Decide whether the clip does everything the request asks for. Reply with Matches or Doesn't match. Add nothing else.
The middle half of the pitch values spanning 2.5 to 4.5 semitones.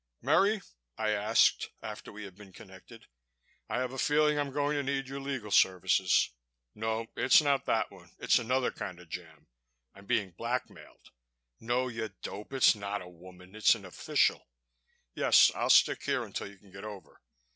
Doesn't match